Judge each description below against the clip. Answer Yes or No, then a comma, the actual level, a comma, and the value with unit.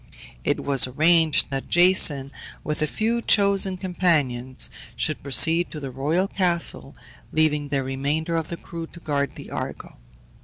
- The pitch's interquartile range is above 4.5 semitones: No, average, 3.9 semitones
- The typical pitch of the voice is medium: Yes, medium, 155 Hz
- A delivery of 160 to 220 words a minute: No, average, 150 wpm